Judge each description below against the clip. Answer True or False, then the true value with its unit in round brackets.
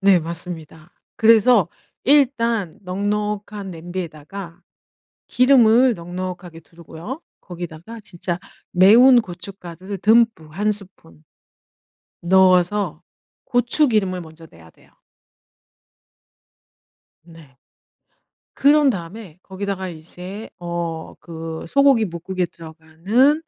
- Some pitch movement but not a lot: True (4.4 semitones)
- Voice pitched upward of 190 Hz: False (185 Hz)